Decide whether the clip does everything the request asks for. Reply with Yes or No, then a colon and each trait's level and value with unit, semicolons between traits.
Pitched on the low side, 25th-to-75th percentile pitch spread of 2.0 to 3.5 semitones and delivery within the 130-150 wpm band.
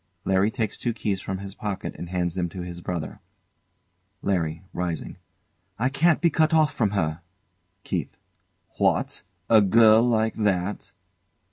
No: low, 100 Hz; average, 4.2 semitones; average, 145 wpm